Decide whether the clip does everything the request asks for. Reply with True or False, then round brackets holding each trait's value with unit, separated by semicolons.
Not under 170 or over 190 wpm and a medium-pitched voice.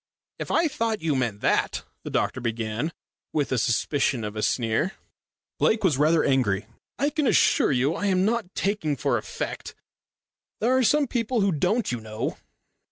True (175 wpm; 155 Hz)